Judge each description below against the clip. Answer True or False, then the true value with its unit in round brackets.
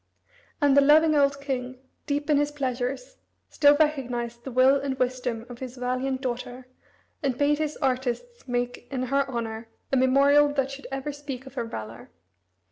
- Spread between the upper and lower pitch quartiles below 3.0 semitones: True (2.4 semitones)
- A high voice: True (265 Hz)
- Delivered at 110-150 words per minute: False (170 wpm)